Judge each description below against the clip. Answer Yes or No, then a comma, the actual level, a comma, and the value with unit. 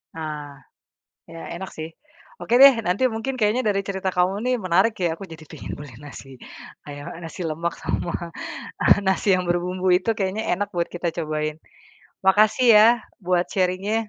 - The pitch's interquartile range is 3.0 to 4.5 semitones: Yes, average, 3.9 semitones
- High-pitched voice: No, medium, 180 Hz